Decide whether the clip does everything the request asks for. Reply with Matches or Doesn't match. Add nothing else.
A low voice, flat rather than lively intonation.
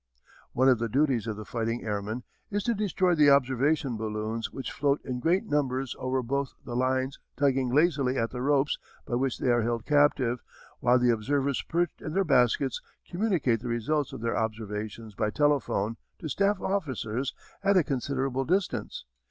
Doesn't match